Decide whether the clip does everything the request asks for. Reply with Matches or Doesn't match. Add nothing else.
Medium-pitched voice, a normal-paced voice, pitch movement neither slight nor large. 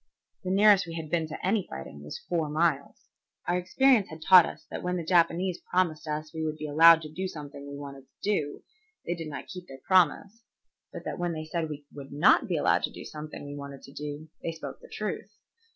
Doesn't match